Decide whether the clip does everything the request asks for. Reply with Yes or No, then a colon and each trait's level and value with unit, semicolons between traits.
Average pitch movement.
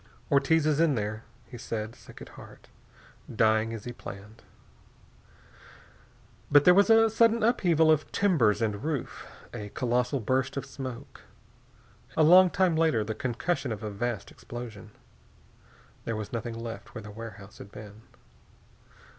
No: wide, 6.3 semitones